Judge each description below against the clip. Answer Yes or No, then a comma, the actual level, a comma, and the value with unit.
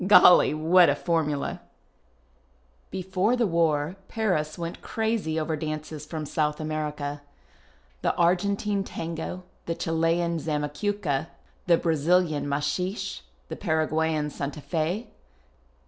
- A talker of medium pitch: Yes, medium, 160 Hz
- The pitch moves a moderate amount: Yes, average, 3.1 semitones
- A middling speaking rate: No, slow, 100 wpm